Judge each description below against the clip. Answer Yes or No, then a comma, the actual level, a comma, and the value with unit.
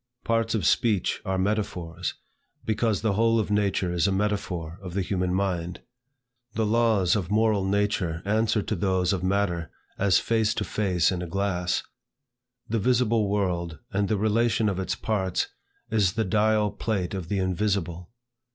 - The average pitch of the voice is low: Yes, low, 100 Hz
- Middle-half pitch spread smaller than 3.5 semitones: Yes, average, 3.0 semitones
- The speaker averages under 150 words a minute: No, average, 160 wpm